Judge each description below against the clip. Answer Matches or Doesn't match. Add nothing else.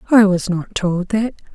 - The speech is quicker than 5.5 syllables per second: Doesn't match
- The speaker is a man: Doesn't match